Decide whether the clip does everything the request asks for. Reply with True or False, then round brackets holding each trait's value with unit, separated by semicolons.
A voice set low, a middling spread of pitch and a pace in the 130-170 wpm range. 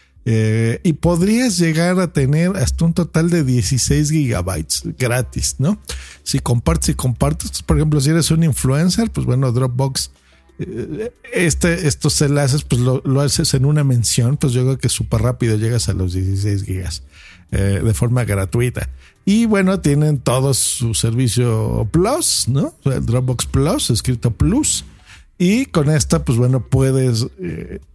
True (130 Hz; 5.0 semitones; 160 wpm)